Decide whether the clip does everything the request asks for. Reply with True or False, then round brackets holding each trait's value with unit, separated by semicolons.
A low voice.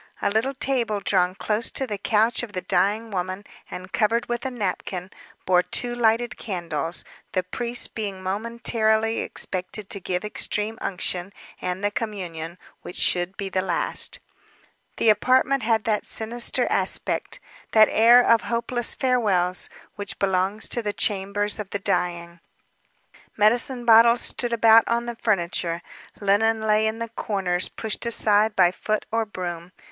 False (210 Hz)